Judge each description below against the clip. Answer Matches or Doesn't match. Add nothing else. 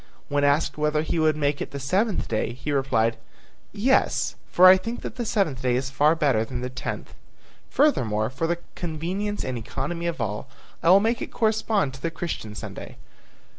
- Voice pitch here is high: Doesn't match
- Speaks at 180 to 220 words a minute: Matches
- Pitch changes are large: Matches